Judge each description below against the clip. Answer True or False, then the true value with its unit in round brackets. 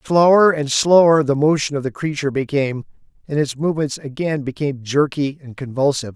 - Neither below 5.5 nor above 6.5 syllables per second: True (5.9 syllables/s)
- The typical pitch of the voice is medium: True (145 Hz)